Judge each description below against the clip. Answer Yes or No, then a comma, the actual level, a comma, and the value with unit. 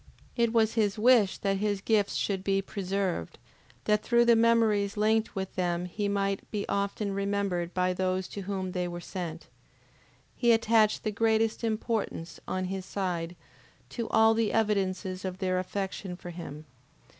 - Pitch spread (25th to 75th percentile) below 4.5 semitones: Yes, average, 2.8 semitones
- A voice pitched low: No, high, 200 Hz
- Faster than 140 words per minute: Yes, average, 160 wpm